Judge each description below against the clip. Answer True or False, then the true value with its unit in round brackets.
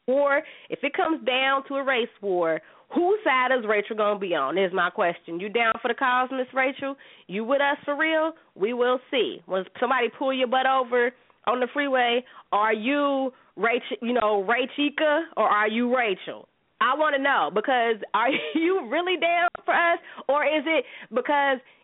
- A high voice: True (260 Hz)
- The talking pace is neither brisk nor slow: True (185 wpm)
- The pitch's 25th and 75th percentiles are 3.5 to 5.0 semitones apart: True (4.0 semitones)